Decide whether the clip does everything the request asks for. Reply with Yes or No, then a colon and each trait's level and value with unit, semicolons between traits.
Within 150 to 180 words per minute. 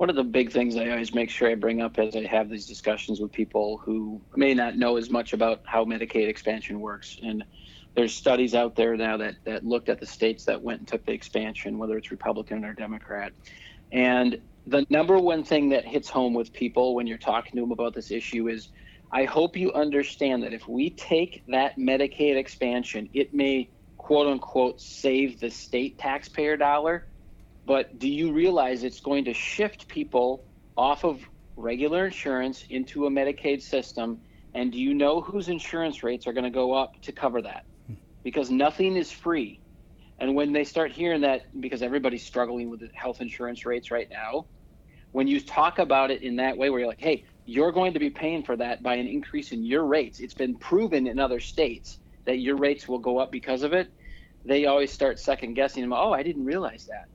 No: fast, 205 wpm